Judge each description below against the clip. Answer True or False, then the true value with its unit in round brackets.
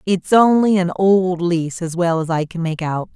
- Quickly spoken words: True (230 wpm)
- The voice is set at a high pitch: False (175 Hz)